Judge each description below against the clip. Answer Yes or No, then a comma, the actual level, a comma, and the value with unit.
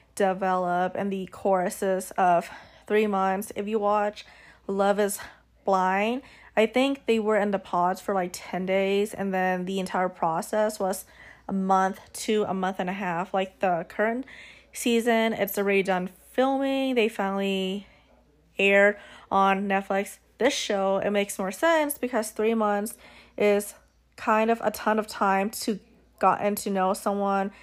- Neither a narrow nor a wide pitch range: No, narrow, 2.1 semitones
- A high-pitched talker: Yes, high, 200 Hz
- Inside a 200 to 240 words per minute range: No, average, 155 wpm